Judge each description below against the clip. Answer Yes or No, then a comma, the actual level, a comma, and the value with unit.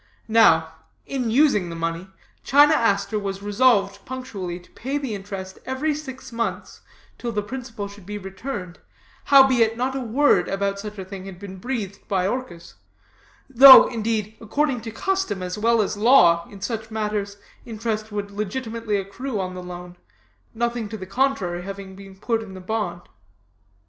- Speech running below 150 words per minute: No, average, 165 wpm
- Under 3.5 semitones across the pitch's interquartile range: No, average, 3.8 semitones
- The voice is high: Yes, high, 210 Hz